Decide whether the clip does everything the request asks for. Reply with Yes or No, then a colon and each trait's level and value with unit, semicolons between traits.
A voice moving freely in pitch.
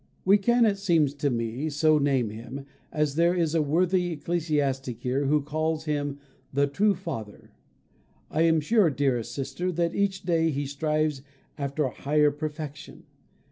No: average, 3.2 semitones